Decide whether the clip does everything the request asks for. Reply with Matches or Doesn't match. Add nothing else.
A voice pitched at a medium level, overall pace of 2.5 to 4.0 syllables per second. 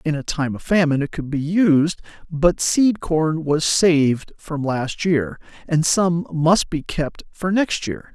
Matches